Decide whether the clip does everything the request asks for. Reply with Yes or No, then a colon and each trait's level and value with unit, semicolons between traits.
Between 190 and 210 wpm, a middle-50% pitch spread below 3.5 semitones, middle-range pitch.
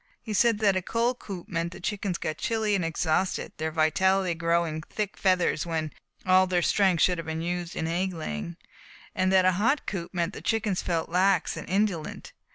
Yes: average, 200 wpm; average, 2.9 semitones; medium, 180 Hz